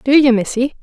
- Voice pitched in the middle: No, very high, 255 Hz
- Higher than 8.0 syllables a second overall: No, 5.3 syllables/s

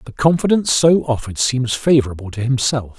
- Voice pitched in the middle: No, low, 130 Hz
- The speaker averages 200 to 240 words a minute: No, average, 160 wpm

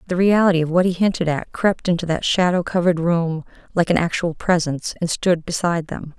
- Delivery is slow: No, fast, 205 wpm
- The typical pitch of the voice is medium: Yes, medium, 170 Hz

